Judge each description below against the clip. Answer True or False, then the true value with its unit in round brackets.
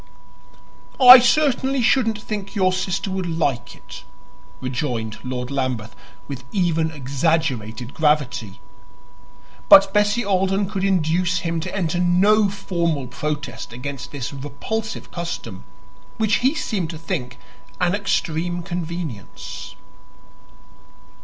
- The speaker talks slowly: True (110 wpm)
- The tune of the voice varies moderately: False (6.0 semitones)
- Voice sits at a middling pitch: True (170 Hz)